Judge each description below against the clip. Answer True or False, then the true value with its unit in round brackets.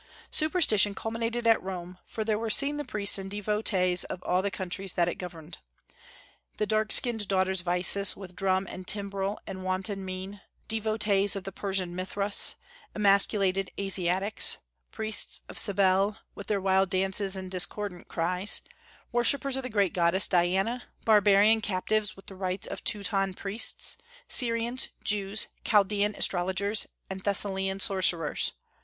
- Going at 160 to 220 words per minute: False (145 wpm)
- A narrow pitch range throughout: True (2.1 semitones)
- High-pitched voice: True (195 Hz)